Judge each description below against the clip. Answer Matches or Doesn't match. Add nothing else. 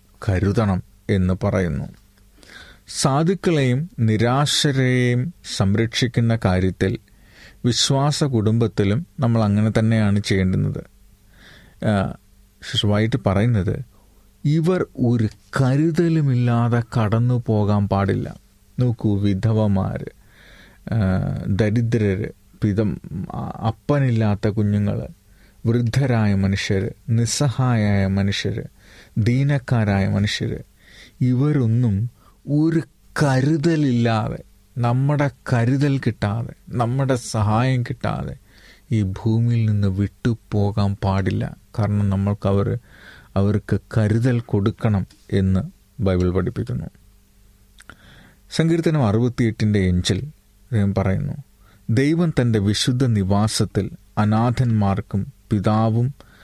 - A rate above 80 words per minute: Doesn't match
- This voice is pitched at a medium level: Doesn't match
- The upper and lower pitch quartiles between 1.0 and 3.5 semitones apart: Doesn't match